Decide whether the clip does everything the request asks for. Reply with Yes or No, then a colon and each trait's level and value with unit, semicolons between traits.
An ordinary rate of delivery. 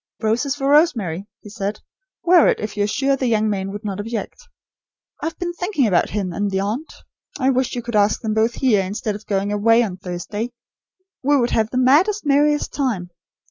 No: fast, 210 wpm